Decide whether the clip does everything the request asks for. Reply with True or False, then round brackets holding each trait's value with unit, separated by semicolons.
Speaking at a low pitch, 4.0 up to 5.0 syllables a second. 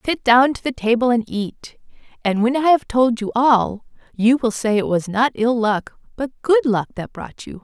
False (240 Hz; 4.6 syllables/s)